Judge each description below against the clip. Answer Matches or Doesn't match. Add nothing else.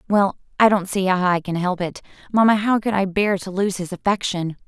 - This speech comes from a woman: Matches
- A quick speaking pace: Matches